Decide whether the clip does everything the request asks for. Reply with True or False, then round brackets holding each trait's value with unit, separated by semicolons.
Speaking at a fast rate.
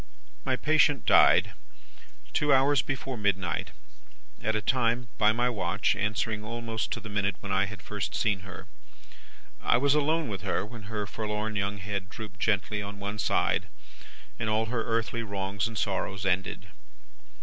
False (160 wpm)